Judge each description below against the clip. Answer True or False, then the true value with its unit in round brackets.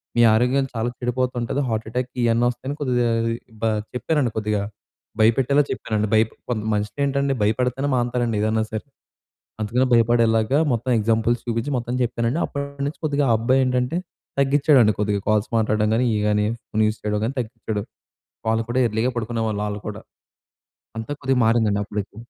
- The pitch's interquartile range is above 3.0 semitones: False (2.7 semitones)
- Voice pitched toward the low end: True (115 Hz)